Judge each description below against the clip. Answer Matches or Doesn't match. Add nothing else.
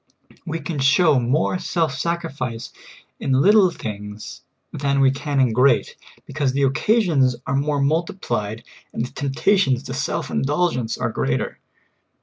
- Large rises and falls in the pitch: Doesn't match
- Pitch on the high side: Doesn't match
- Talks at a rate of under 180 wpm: Matches